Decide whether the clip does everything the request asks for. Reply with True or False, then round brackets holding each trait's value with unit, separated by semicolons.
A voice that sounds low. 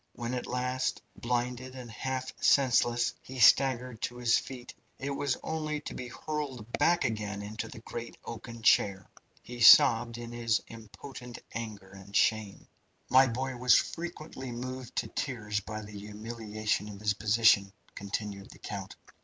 True (120 Hz)